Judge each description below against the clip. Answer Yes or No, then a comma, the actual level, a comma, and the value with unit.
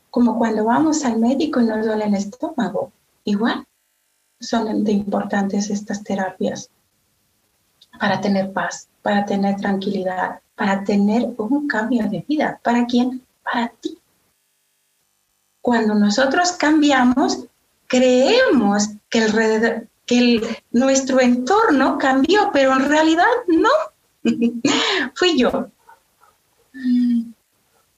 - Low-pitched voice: No, high, 240 Hz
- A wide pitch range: No, average, 4.0 semitones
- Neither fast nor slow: No, slow, 105 wpm